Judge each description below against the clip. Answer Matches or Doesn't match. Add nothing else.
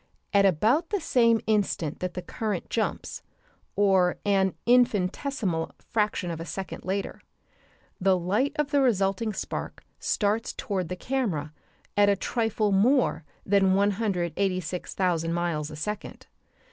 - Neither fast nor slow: Doesn't match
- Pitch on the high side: Matches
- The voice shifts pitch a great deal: Doesn't match